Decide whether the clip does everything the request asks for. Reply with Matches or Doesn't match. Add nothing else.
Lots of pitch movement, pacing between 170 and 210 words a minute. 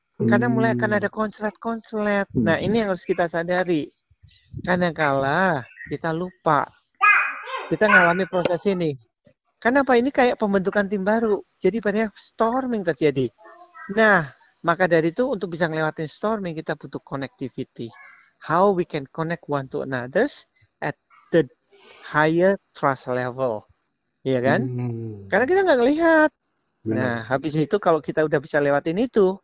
Doesn't match